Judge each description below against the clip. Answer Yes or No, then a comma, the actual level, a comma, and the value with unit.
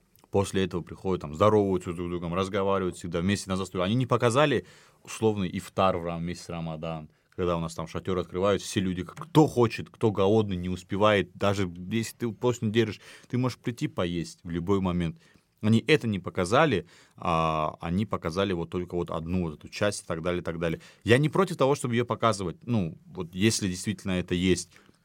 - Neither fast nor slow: No, fast, 195 wpm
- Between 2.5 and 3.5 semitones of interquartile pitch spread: No, average, 4.2 semitones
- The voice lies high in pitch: No, very low, 95 Hz